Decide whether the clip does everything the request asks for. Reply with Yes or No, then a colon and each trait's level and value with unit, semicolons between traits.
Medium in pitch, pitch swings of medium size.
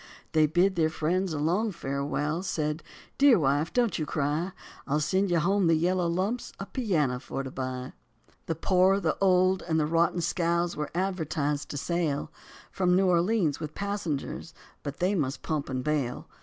Yes: medium, 170 Hz; average, 3.8 semitones